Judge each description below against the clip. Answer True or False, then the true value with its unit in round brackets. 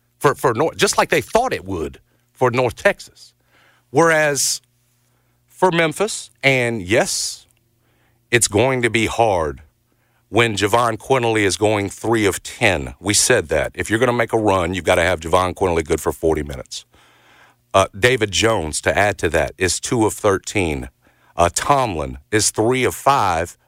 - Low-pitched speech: True (115 Hz)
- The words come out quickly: False (170 wpm)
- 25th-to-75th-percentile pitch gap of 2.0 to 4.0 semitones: True (3.5 semitones)